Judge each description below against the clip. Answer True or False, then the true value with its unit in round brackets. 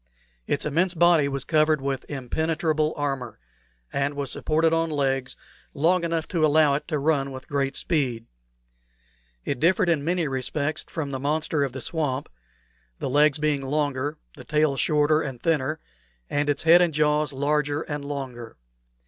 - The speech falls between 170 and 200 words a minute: False (160 wpm)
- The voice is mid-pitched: True (150 Hz)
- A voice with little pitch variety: True (2.3 semitones)